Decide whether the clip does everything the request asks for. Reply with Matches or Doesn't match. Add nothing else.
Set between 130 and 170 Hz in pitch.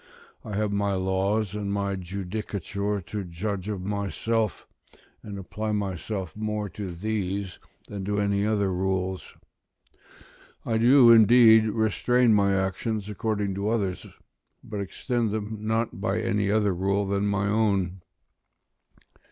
Doesn't match